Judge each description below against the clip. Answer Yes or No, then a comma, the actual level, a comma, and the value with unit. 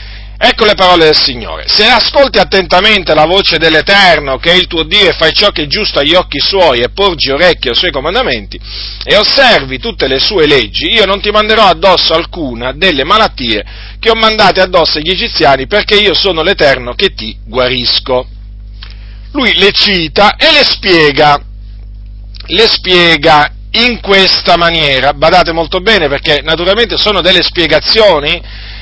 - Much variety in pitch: Yes, wide, 7.3 semitones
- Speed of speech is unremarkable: Yes, average, 160 wpm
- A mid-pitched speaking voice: Yes, medium, 165 Hz